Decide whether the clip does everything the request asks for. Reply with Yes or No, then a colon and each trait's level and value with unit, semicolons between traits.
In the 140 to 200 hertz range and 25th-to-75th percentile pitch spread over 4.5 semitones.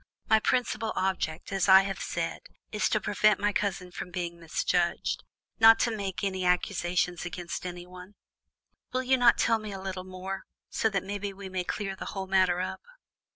No: high, 190 Hz; narrow, 2.4 semitones